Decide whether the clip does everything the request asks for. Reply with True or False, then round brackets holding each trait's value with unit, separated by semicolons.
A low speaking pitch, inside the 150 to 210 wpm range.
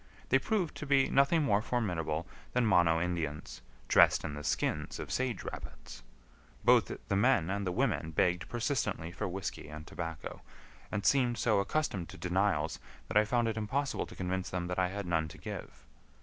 True (95 Hz; 180 wpm)